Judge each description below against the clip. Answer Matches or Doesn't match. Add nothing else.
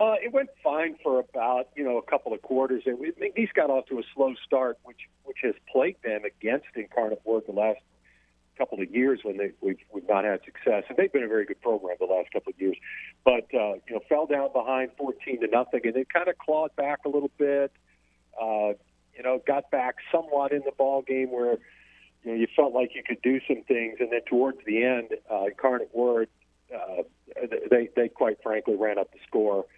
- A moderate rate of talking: Doesn't match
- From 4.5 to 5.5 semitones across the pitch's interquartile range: Matches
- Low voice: Matches